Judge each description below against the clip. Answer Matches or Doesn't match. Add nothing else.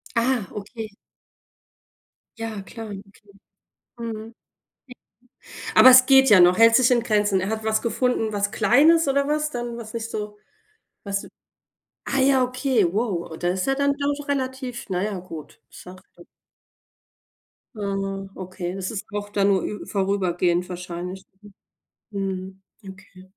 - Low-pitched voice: Doesn't match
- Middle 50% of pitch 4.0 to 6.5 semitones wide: Matches